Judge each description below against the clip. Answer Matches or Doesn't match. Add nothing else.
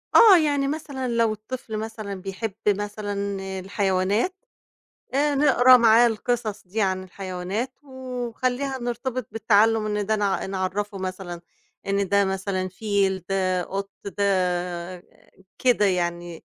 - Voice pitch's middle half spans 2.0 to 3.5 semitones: Doesn't match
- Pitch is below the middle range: Doesn't match